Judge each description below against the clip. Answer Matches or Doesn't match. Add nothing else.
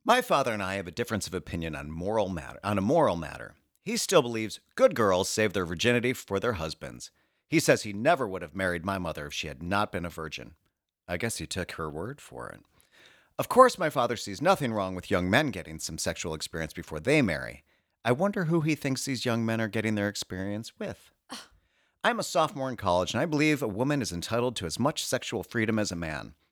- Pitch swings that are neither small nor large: Doesn't match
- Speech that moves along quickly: Matches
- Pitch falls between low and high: Doesn't match